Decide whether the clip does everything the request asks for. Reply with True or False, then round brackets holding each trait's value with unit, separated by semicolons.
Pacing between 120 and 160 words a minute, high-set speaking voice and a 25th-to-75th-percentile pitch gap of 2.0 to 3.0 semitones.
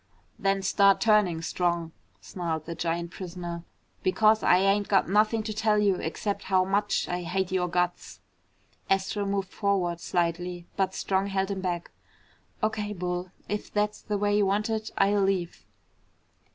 True (155 wpm; 195 Hz; 2.6 semitones)